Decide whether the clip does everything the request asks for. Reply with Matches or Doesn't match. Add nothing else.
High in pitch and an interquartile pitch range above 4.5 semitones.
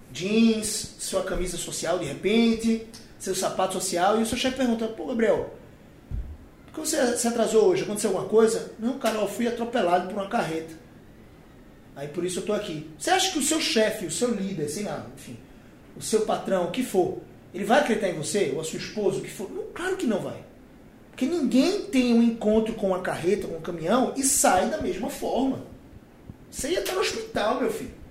Matches